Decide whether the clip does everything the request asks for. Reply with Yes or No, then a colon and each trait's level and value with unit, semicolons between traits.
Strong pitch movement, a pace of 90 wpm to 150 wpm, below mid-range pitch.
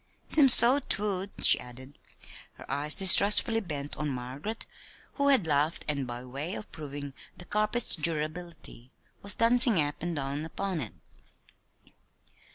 No: wide, 6.6 semitones; average, 140 wpm; medium, 160 Hz